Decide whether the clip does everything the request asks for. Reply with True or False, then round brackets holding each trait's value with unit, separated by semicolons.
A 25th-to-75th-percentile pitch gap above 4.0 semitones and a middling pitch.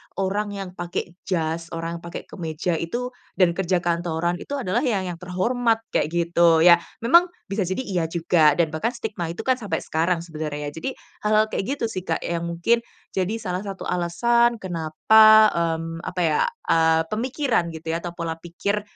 True (4.4 semitones; 175 Hz)